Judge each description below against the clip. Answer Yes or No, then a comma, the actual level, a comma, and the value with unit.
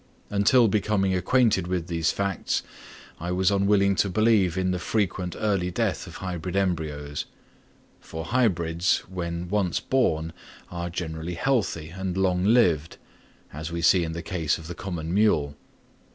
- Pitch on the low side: Yes, very low, 90 Hz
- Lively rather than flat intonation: No, average, 2.9 semitones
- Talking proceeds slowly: No, average, 150 wpm